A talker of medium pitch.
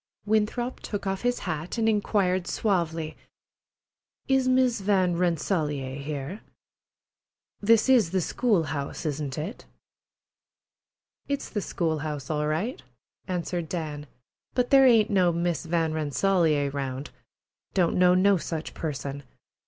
Yes: medium, 175 Hz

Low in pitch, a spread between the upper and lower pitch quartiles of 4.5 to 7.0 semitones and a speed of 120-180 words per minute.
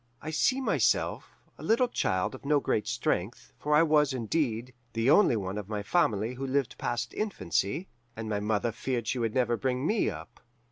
No: low, 125 Hz; wide, 5.5 semitones; average, 190 wpm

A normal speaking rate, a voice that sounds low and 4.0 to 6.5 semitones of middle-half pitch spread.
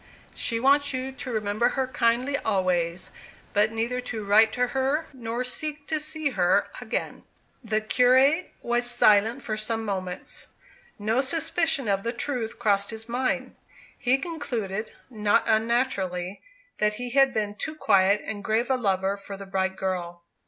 No: average, 155 wpm; high, 230 Hz; average, 4.3 semitones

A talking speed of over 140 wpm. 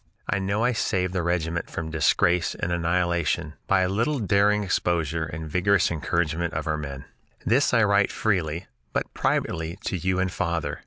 Yes: average, 170 wpm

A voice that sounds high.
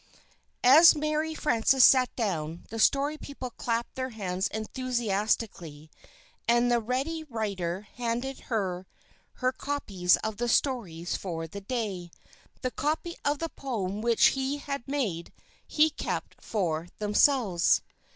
Yes: high, 235 Hz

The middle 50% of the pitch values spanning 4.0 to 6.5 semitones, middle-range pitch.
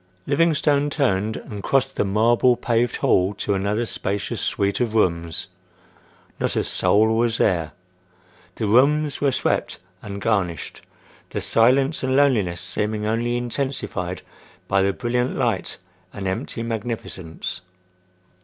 No: average, 4.4 semitones; low, 110 Hz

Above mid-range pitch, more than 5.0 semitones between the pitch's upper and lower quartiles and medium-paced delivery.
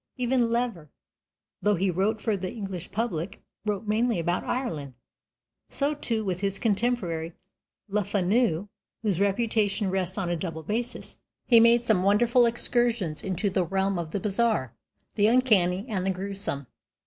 No: high, 200 Hz; average, 4.2 semitones; average, 150 wpm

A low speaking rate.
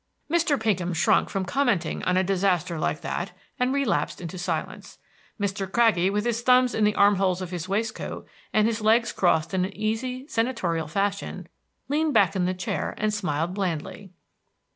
No: average, 175 wpm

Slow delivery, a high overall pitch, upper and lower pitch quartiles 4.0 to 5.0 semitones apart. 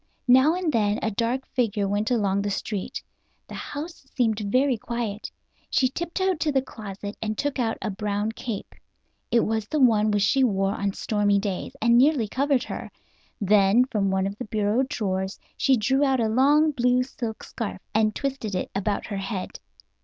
No: average, 180 wpm; high, 220 Hz; average, 4.3 semitones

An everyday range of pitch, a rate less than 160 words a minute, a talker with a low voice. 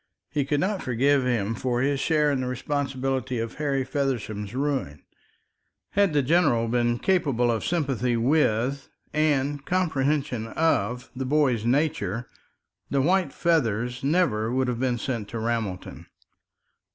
Yes: average, 3.7 semitones; average, 140 wpm; low, 130 Hz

